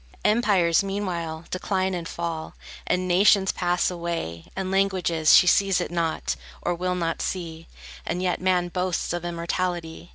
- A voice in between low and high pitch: Yes, medium, 175 Hz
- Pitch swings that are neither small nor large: No, narrow, 1.8 semitones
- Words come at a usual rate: Yes, average, 150 wpm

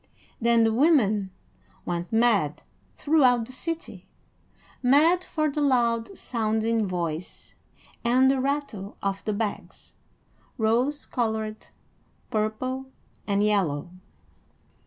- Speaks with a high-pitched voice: Yes, high, 230 Hz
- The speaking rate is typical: No, slow, 100 wpm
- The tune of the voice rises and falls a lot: No, average, 4.1 semitones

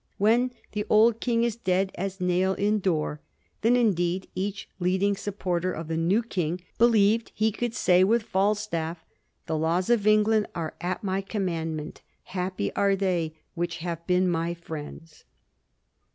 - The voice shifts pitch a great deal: No, average, 3.7 semitones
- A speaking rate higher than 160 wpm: No, average, 155 wpm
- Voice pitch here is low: No, medium, 185 Hz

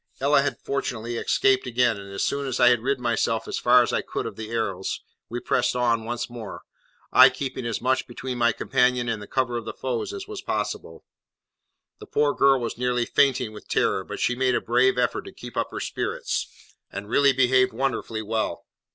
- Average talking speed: No, fast, 210 wpm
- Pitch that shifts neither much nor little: No, narrow, 2.1 semitones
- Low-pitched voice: Yes, low, 125 Hz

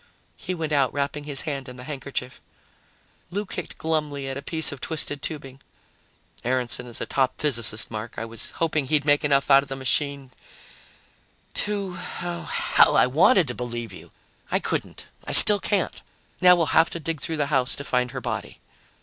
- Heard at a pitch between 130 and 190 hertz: Yes, medium, 140 Hz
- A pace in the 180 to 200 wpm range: Yes, average, 185 wpm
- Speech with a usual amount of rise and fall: Yes, average, 3.8 semitones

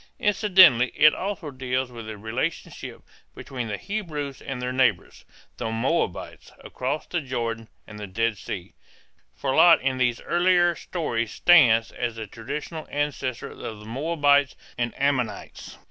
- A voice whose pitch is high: No, low, 130 Hz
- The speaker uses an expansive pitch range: No, average, 5.0 semitones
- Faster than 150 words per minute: No, average, 145 wpm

